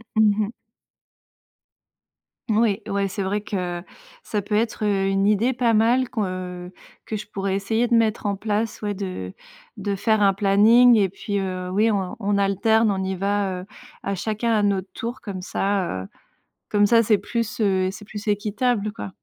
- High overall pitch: Yes, high, 205 Hz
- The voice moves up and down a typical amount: No, narrow, 2.1 semitones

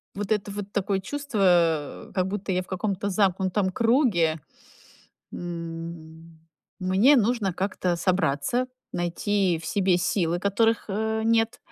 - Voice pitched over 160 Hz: Yes, high, 190 Hz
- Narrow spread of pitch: No, average, 3.2 semitones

